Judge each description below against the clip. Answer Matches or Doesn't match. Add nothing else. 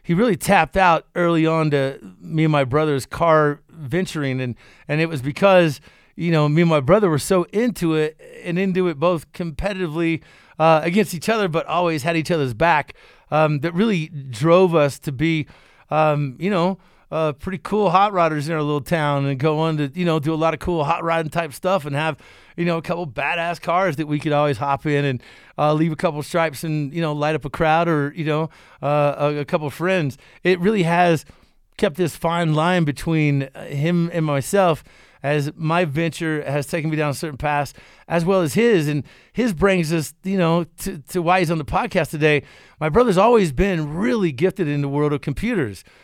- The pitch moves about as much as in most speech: Matches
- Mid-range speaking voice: Matches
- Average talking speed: Doesn't match